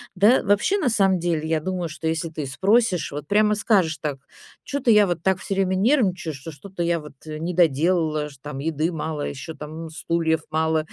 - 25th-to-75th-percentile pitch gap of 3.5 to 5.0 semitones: Yes, average, 3.8 semitones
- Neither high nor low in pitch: Yes, medium, 165 Hz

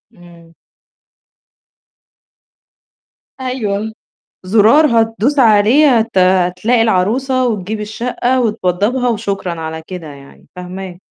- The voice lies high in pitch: Yes, high, 210 Hz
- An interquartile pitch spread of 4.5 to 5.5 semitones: Yes, average, 4.8 semitones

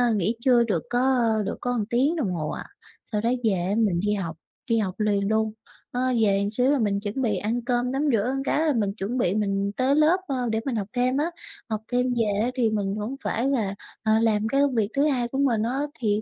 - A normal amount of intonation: Yes, average, 3.5 semitones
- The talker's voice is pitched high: Yes, high, 225 Hz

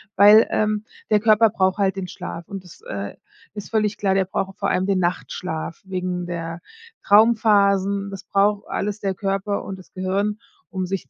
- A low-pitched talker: No, high, 195 Hz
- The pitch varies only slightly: Yes, narrow, 1.9 semitones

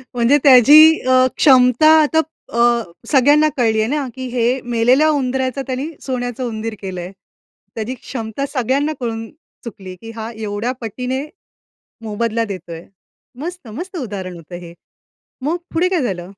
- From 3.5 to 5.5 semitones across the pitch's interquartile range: Yes, average, 3.8 semitones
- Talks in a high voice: Yes, high, 245 Hz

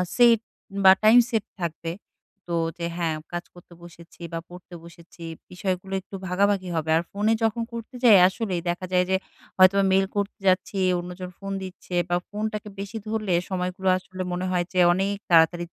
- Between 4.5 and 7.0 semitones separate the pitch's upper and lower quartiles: No, narrow, 2.5 semitones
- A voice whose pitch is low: No, medium, 185 Hz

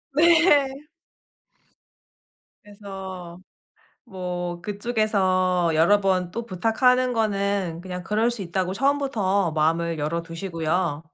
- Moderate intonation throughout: Yes, average, 4.2 semitones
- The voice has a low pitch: No, high, 190 Hz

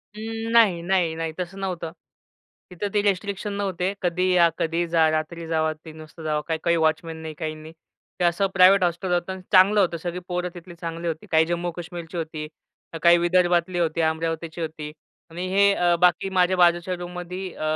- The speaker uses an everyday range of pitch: No, narrow, 2.1 semitones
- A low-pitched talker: No, medium, 175 Hz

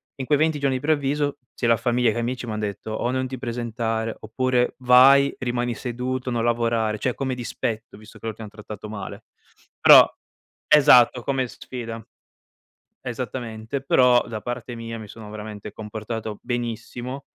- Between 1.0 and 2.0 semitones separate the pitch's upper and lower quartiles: No, narrow, 2.4 semitones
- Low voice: Yes, low, 120 Hz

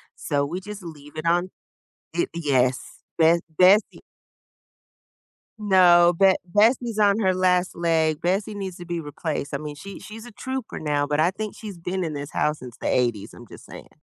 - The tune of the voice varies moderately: Yes, average, 4.5 semitones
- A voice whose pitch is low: No, medium, 175 Hz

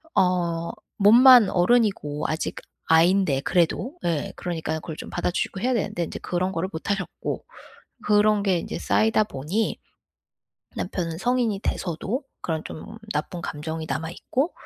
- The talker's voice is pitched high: No, medium, 180 Hz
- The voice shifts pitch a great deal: No, average, 4.5 semitones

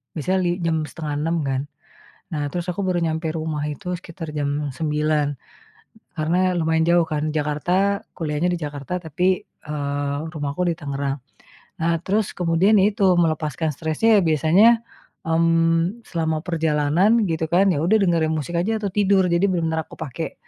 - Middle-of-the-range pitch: Yes, medium, 165 Hz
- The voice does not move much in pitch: No, average, 3.1 semitones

